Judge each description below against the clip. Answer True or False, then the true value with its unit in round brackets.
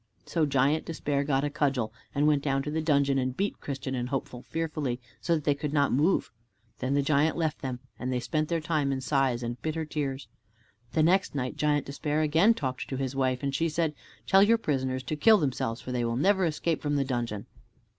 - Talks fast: True (220 wpm)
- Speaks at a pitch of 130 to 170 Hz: True (140 Hz)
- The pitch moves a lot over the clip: False (3.0 semitones)